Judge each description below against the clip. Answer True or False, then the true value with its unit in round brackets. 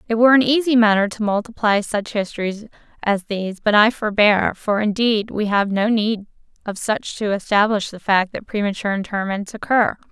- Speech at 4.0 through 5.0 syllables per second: False (5.3 syllables/s)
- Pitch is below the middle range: False (210 Hz)